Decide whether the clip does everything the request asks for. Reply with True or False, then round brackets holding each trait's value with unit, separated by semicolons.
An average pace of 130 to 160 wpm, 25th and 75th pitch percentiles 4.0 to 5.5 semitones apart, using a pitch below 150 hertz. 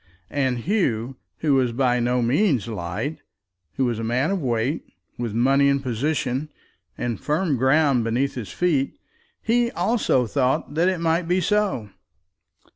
True (150 wpm; 4.9 semitones; 135 Hz)